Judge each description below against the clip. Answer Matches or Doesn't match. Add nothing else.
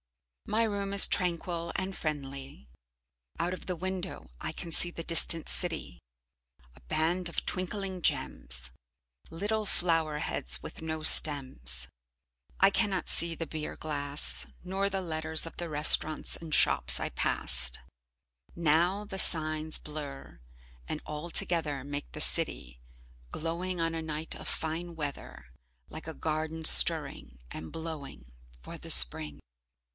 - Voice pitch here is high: Doesn't match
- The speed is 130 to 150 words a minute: Matches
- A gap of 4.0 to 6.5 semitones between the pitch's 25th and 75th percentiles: Doesn't match